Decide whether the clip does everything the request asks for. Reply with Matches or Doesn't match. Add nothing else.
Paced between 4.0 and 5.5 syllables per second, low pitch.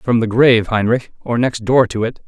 Matches